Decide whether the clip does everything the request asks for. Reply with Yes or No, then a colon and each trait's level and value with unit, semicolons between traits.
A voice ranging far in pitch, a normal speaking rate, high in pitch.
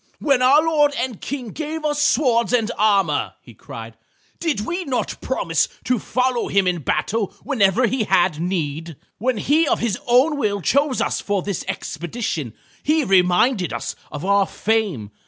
Yes: wide, 6.7 semitones; average, 165 wpm; high, 225 Hz